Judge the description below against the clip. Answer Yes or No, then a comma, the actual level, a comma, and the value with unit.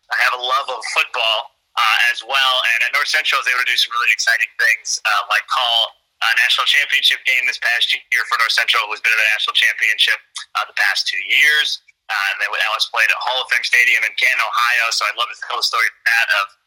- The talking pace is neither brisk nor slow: No, fast, 250 wpm